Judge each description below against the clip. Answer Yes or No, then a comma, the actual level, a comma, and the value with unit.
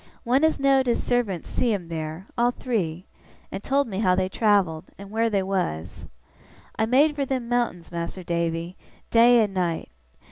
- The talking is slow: No, average, 175 wpm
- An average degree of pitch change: No, wide, 5.9 semitones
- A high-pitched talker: Yes, high, 200 Hz